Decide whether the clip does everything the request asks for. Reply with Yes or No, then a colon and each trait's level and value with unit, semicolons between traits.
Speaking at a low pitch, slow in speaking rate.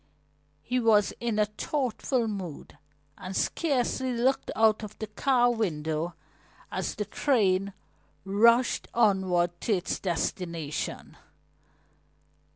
No: high, 210 Hz; slow, 105 wpm